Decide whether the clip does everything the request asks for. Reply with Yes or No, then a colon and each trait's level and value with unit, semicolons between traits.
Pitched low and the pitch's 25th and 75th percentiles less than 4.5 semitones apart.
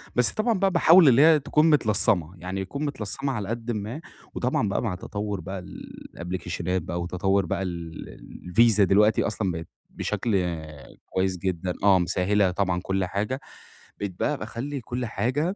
No: low, 100 Hz; average, 5.2 semitones